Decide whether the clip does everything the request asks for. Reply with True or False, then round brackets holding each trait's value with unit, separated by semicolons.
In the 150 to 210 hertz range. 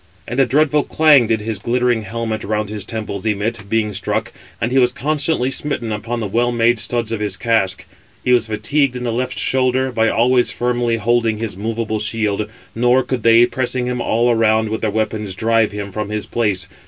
False (115 Hz)